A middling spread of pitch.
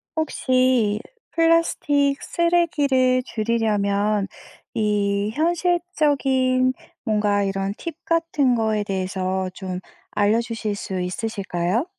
No: wide, 5.9 semitones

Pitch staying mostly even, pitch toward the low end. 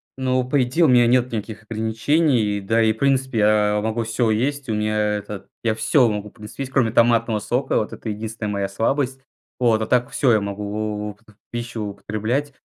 No: average, 3.0 semitones; low, 110 Hz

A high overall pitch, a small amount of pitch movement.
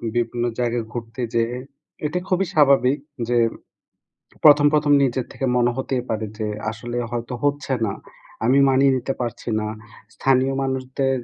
No: low, 130 Hz; narrow, 2.3 semitones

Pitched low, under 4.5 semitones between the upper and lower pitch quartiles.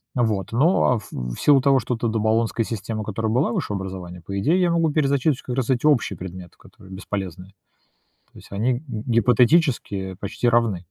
No: low, 115 Hz; average, 4.9 semitones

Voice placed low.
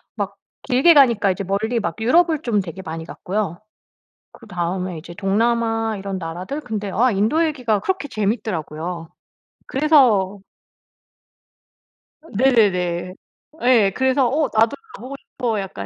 No: high, 215 Hz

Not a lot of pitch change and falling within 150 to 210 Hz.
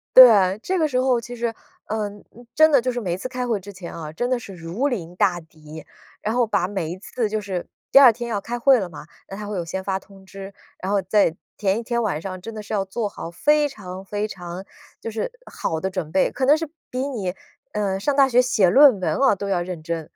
No: average, 4.7 semitones; high, 205 Hz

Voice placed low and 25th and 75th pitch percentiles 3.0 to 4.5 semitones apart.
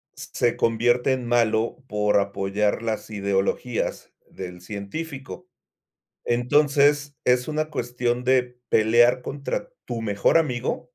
Yes: low, 120 Hz; average, 3.8 semitones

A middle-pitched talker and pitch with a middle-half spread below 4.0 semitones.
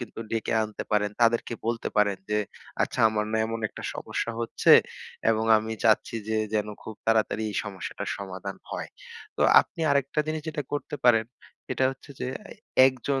No: low, 110 Hz; narrow, 2.5 semitones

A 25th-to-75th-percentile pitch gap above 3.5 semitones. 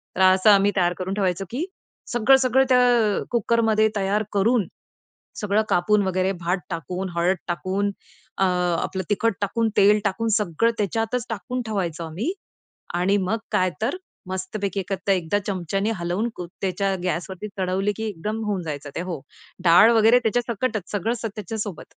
No: average, 3.2 semitones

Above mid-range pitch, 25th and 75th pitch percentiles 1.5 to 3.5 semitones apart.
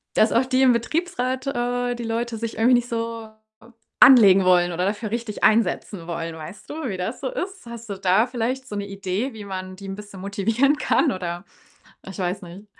No: high, 220 Hz; average, 4.3 semitones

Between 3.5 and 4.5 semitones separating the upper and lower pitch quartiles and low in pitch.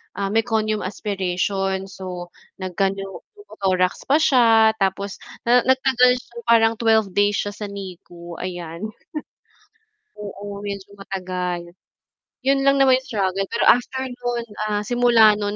No: average, 3.9 semitones; high, 205 Hz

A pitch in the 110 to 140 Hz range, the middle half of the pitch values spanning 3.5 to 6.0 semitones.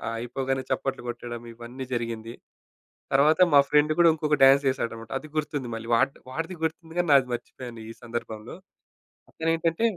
Yes: low, 135 Hz; average, 4.6 semitones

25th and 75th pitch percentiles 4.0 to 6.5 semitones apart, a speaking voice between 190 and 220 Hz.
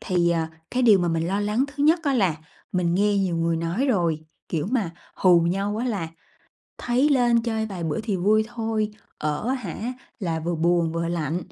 Yes: wide, 5.4 semitones; high, 195 Hz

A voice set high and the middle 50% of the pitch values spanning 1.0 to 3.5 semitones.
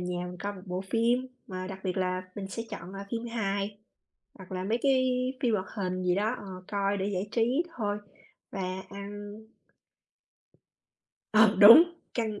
Yes: high, 200 Hz; average, 3.0 semitones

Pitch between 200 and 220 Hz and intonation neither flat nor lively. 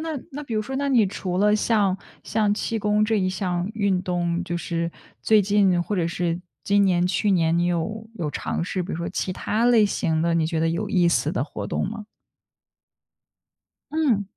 No: high, 190 Hz; average, 3.6 semitones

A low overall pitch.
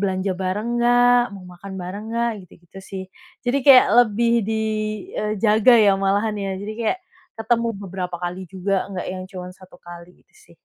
No: high, 200 Hz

